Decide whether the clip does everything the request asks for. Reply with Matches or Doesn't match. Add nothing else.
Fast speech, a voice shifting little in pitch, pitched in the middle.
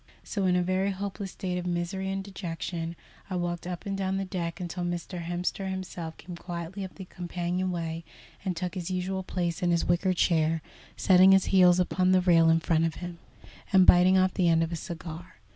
Matches